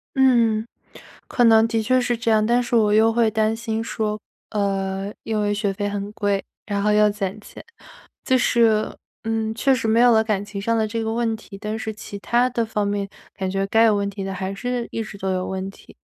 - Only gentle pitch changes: Yes, narrow, 2.1 semitones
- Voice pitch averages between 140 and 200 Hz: No, high, 215 Hz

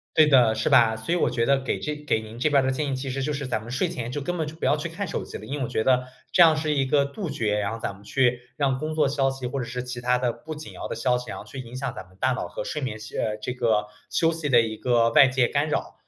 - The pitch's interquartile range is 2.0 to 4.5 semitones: Yes, average, 3.9 semitones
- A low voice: Yes, low, 130 Hz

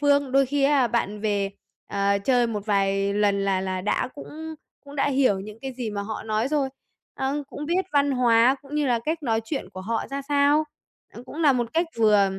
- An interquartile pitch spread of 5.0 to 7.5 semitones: Yes, wide, 5.5 semitones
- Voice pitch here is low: No, high, 245 Hz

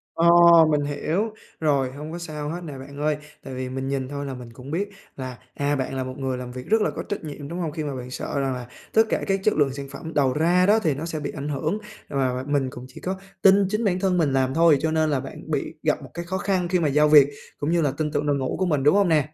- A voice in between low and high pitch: Yes, medium, 150 Hz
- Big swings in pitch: No, average, 4.0 semitones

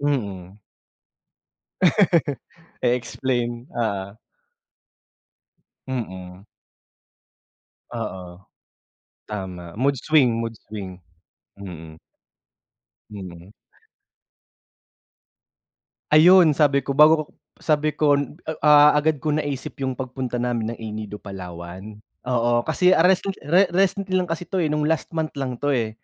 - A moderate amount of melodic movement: No, wide, 7.0 semitones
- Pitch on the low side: Yes, low, 125 Hz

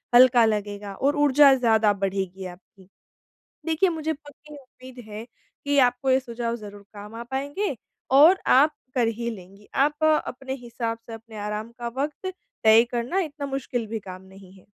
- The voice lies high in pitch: Yes, high, 240 Hz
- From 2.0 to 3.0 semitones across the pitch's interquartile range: No, average, 5.2 semitones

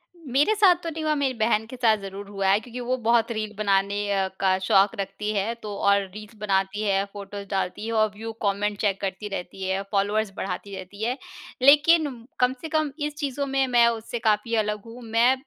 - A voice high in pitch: Yes, high, 215 Hz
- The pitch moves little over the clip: No, average, 4.0 semitones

